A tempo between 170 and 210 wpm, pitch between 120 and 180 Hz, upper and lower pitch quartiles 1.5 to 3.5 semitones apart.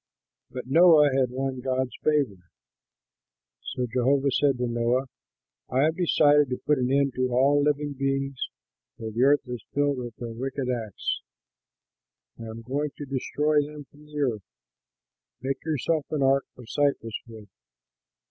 No: average, 155 wpm; low, 135 Hz; average, 2.8 semitones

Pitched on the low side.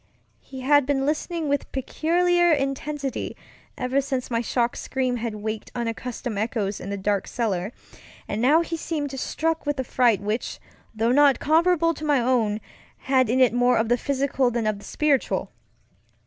No: very high, 260 Hz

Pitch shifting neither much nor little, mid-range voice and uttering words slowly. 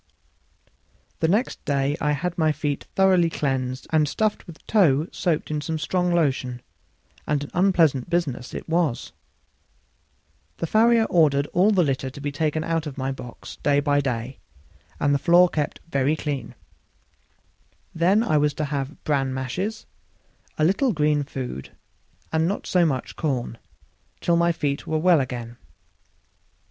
No: average, 3.8 semitones; medium, 150 Hz; average, 155 wpm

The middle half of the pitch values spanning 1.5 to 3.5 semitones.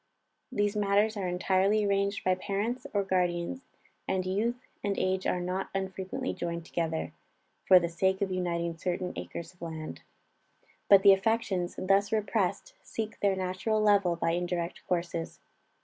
Yes: narrow, 2.4 semitones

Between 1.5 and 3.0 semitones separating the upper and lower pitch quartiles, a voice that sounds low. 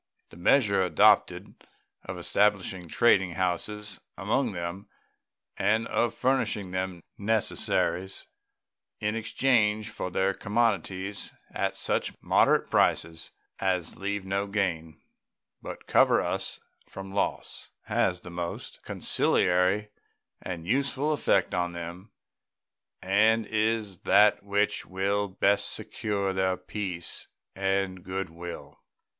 Yes: narrow, 2.4 semitones; very low, 95 Hz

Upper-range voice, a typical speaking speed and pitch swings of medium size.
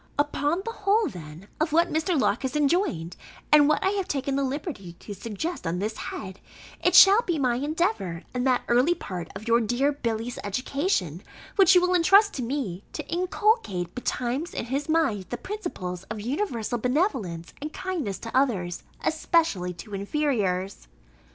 No: very high, 260 Hz; average, 170 wpm; wide, 8.7 semitones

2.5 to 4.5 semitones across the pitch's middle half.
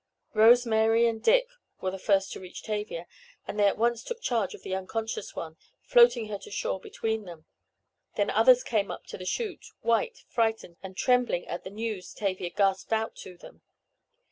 Yes: average, 3.6 semitones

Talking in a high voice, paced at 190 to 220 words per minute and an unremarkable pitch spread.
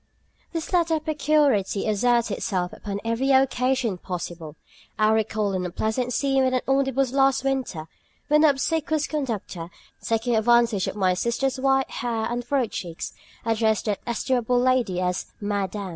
No: high, 240 Hz; average, 145 wpm; average, 4.8 semitones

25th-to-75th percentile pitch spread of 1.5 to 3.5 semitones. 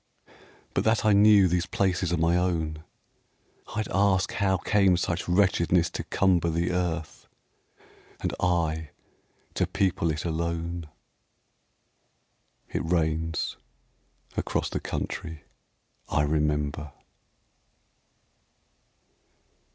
Yes: narrow, 2.6 semitones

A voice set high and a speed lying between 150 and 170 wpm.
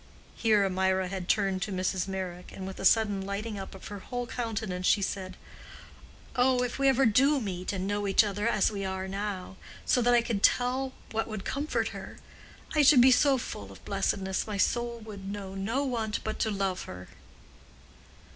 No: high, 205 Hz; average, 190 wpm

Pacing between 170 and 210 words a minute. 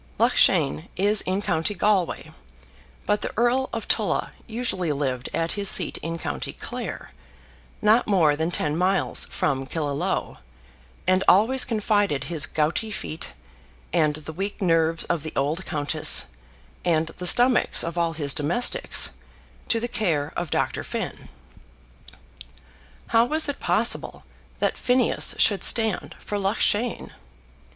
No: slow, 135 wpm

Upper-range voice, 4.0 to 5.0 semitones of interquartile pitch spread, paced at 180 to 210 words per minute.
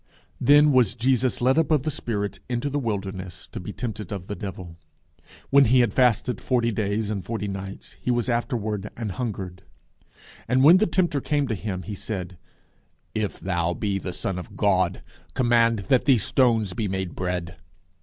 No: low, 110 Hz; average, 4.7 semitones; average, 185 wpm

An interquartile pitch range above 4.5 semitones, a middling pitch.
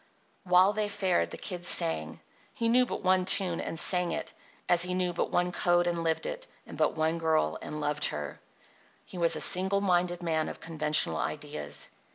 No: narrow, 2.5 semitones; medium, 175 Hz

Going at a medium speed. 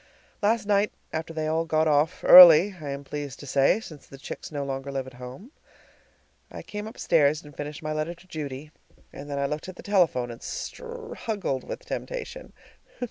Yes: average, 190 wpm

